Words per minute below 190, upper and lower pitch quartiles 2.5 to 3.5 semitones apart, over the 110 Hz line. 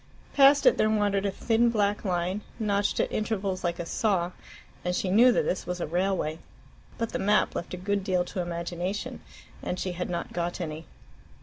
No: average, 195 wpm; average, 3.0 semitones; high, 190 Hz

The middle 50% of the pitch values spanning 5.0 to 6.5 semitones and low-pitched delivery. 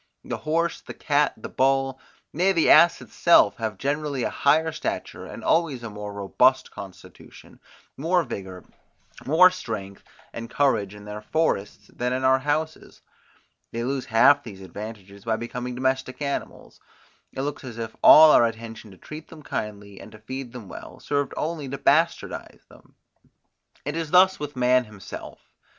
Yes: wide, 5.4 semitones; low, 130 Hz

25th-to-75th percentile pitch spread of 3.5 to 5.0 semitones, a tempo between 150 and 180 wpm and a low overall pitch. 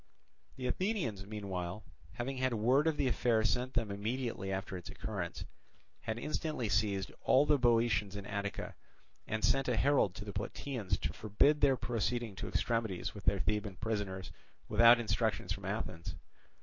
Yes: average, 3.8 semitones; average, 160 wpm; low, 110 Hz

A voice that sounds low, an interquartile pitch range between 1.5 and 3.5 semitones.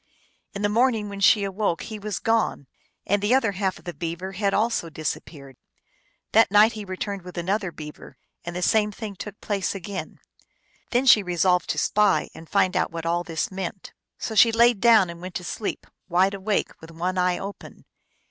No: high, 195 Hz; average, 3.1 semitones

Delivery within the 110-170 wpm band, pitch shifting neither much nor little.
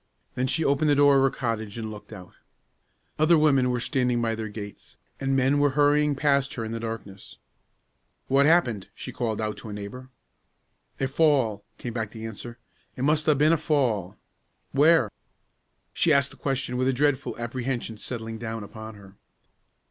No: average, 180 wpm; average, 4.2 semitones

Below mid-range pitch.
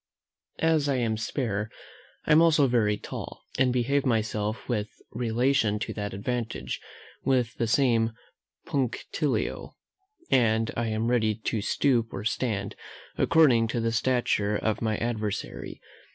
Yes: low, 115 Hz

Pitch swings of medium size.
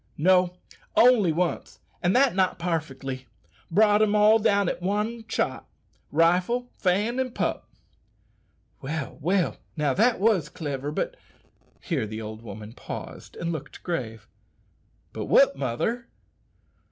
No: wide, 7.0 semitones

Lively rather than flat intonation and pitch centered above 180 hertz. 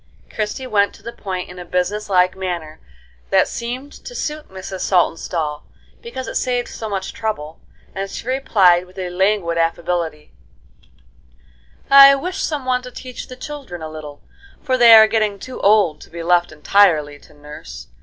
Yes: wide, 6.3 semitones; high, 190 Hz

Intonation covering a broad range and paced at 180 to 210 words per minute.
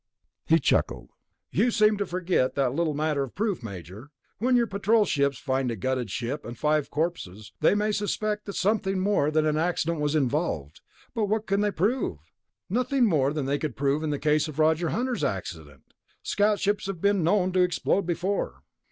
Yes: wide, 6.5 semitones; average, 190 wpm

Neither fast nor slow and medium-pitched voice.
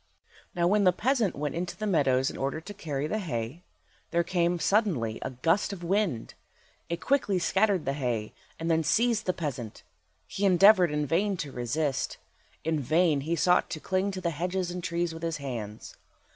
Yes: average, 185 wpm; medium, 170 Hz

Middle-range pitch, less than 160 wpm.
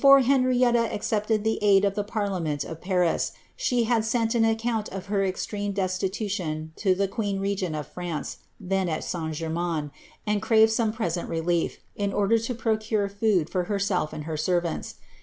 No: high, 200 Hz; average, 140 wpm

